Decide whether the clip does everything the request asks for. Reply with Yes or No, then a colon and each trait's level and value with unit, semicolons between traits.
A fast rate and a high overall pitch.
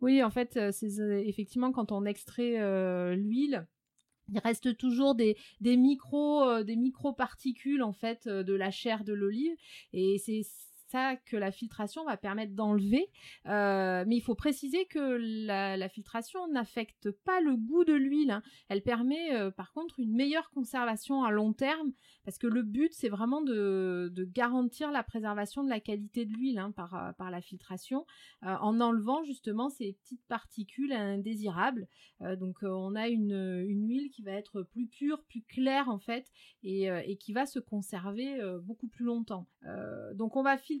No: average, 180 wpm; high, 230 Hz